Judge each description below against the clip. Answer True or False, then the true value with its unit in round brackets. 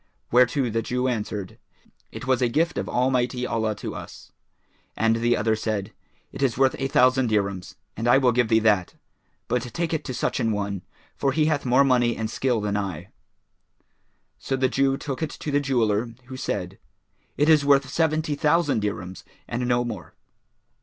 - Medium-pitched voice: False (125 Hz)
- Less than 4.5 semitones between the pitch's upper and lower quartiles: True (3.7 semitones)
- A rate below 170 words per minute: False (185 wpm)